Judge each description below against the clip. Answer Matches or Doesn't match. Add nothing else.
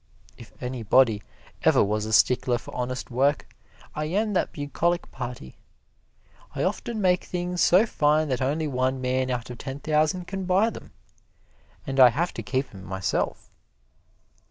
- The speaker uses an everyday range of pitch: Doesn't match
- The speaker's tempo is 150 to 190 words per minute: Matches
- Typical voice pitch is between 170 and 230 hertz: Doesn't match